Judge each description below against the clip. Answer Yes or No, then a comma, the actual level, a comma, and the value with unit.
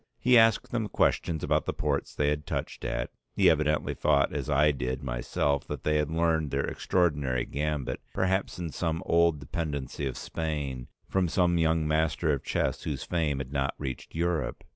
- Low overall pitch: Yes, very low, 75 Hz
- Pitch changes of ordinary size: Yes, average, 3.1 semitones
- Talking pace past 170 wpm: Yes, average, 180 wpm